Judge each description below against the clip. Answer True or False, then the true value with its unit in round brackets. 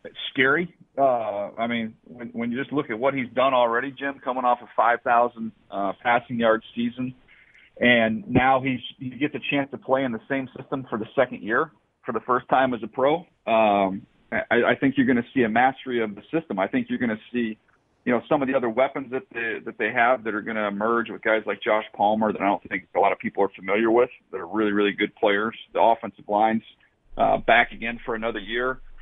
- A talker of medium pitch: False (120 Hz)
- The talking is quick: True (235 wpm)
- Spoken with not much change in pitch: False (3.3 semitones)